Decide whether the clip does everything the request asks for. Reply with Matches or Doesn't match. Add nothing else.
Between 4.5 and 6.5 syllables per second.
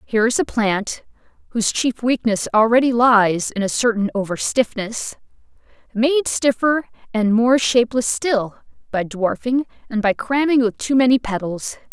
Doesn't match